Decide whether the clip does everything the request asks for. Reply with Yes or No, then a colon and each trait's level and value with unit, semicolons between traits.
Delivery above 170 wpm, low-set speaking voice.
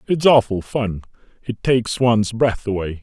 No: average, 160 wpm; low, 115 Hz